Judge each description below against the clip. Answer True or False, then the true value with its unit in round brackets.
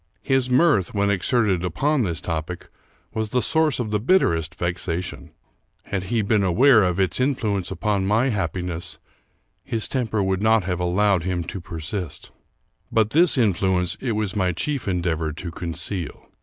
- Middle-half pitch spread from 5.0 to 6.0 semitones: False (4.3 semitones)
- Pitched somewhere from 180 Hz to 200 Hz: False (100 Hz)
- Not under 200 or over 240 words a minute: False (160 wpm)